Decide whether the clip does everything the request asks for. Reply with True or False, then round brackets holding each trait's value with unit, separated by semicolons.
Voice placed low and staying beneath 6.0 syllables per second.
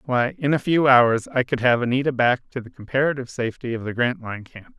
False (130 Hz; 6.1 syllables/s)